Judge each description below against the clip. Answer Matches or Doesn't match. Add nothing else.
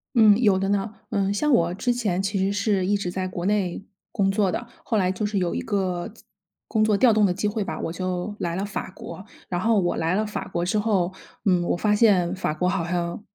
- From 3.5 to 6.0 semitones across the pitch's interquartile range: Doesn't match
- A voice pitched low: Doesn't match